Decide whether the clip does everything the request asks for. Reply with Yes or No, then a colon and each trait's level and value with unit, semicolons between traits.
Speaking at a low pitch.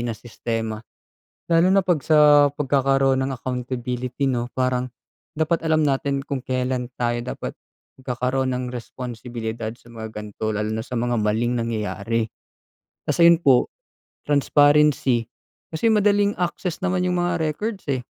Yes: low, 130 Hz